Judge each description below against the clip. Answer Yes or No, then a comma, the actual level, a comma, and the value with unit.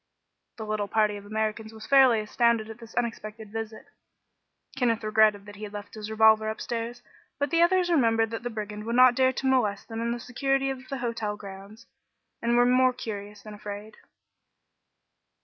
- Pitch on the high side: Yes, high, 225 Hz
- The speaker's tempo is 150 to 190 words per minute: Yes, average, 185 wpm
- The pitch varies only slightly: Yes, narrow, 2.3 semitones